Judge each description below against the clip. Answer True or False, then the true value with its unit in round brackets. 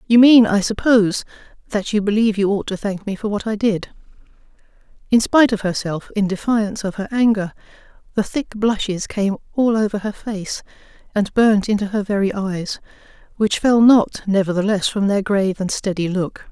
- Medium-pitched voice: False (205 Hz)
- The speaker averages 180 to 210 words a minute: False (170 wpm)